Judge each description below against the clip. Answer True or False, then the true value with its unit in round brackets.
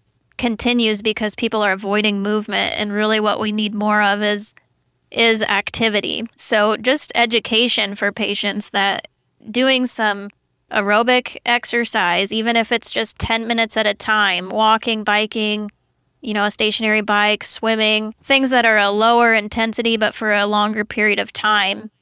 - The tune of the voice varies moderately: False (1.6 semitones)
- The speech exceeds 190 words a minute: False (155 wpm)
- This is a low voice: False (215 Hz)